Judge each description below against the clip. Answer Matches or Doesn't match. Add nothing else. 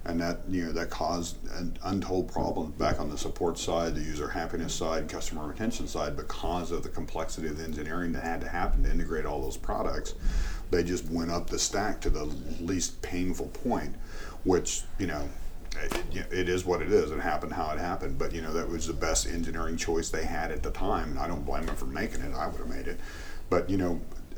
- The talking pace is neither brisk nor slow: Doesn't match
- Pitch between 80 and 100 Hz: Matches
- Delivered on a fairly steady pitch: Matches